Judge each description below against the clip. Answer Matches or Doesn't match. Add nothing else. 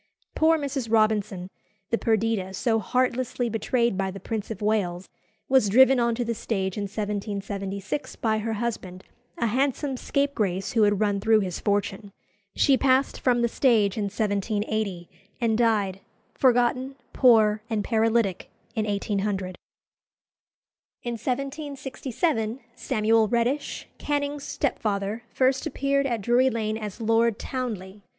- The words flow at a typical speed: Doesn't match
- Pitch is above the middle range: Matches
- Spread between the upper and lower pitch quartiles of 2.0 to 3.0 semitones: Doesn't match